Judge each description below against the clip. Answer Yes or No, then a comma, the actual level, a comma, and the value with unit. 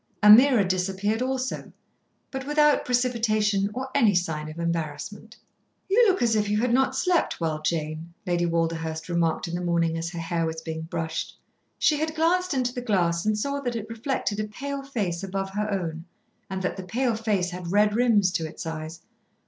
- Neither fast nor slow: Yes, average, 190 wpm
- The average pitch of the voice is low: No, high, 205 Hz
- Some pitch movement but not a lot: No, wide, 6.6 semitones